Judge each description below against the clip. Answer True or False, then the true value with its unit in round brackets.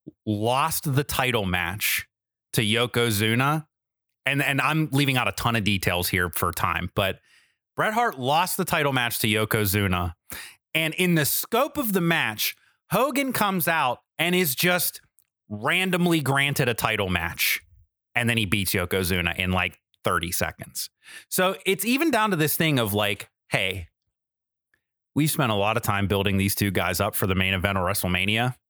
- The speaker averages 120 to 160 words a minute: False (170 wpm)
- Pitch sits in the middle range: False (115 Hz)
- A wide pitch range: True (7.7 semitones)